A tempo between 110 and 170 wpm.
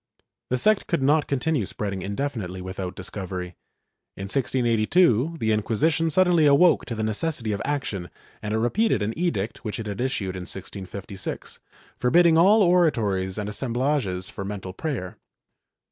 Yes: average, 155 wpm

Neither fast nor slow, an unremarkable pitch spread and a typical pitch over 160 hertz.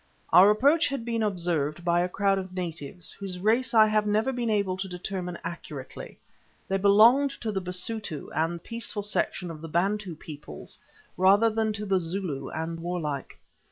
Yes: average, 170 wpm; average, 3.9 semitones; high, 190 Hz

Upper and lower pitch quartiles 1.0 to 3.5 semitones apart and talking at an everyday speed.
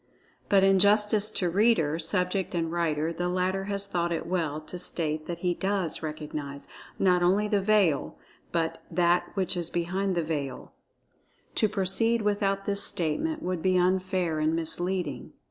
Yes: average, 3.1 semitones; average, 160 wpm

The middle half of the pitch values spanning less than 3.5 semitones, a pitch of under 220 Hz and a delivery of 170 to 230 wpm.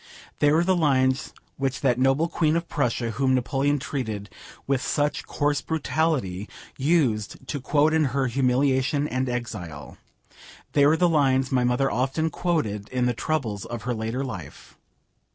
No: average, 3.1 semitones; low, 135 Hz; average, 155 wpm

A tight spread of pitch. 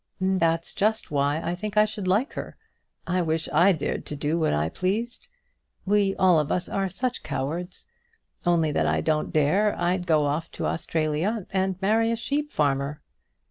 No: average, 4.7 semitones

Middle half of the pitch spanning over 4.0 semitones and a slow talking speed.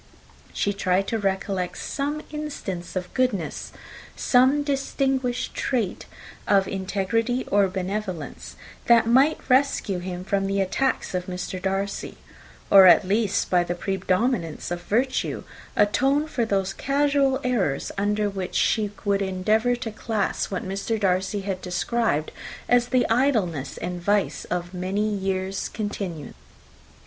Yes: average, 4.6 semitones; slow, 130 wpm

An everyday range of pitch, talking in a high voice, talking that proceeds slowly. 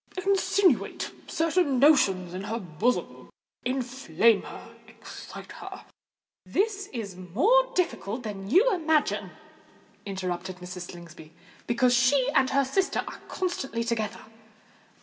No: wide, 8.4 semitones; high, 245 Hz; slow, 105 wpm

